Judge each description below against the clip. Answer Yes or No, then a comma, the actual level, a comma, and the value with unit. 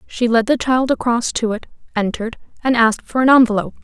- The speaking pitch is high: Yes, high, 235 Hz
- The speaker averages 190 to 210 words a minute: Yes, fast, 205 wpm